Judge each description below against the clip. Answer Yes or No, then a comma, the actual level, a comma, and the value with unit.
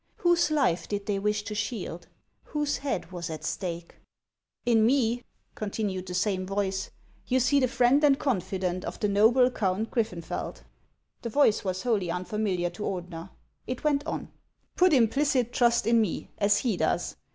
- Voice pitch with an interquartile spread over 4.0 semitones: Yes, average, 5.0 semitones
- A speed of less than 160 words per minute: No, average, 175 wpm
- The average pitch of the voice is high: Yes, high, 210 Hz